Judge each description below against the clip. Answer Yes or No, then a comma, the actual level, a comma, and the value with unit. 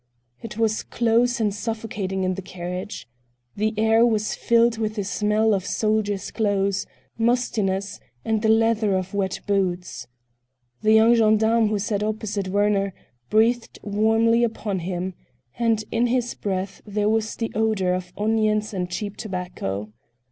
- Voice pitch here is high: Yes, high, 215 Hz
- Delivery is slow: No, average, 145 wpm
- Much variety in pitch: No, narrow, 2.4 semitones